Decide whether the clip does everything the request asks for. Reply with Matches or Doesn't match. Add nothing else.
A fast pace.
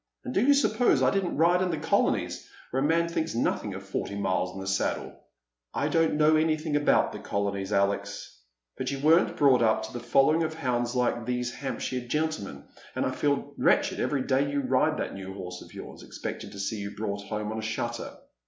Matches